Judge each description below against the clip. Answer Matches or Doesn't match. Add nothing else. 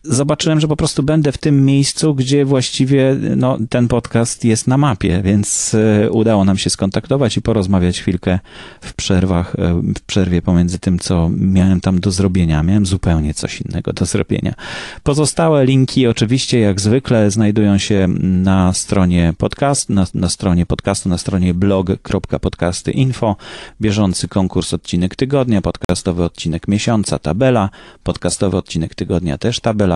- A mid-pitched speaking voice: Doesn't match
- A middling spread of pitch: Doesn't match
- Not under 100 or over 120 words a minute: Doesn't match